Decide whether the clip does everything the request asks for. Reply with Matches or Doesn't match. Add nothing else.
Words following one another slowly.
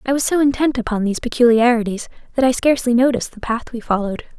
Doesn't match